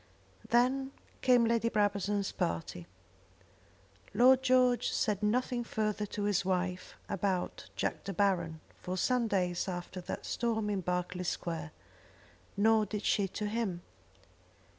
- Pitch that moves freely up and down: No, average, 4.2 semitones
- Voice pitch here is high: Yes, high, 205 Hz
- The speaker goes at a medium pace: No, slow, 125 wpm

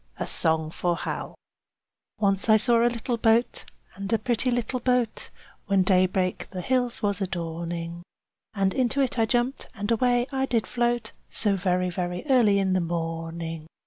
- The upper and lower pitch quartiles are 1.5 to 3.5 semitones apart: No, average, 5.2 semitones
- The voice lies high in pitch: Yes, high, 200 Hz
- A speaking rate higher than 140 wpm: Yes, average, 165 wpm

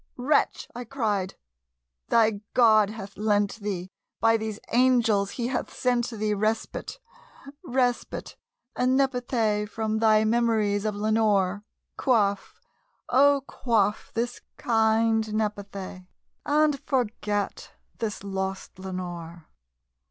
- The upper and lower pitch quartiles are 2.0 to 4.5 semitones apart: Yes, average, 2.9 semitones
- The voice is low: No, high, 220 Hz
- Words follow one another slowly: Yes, slow, 105 wpm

